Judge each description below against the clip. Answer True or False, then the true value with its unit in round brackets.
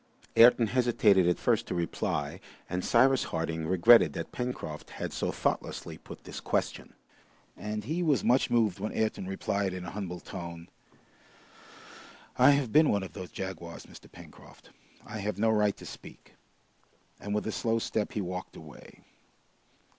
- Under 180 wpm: True (160 wpm)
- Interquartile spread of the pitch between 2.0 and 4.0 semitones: False (4.5 semitones)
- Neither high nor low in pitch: False (105 Hz)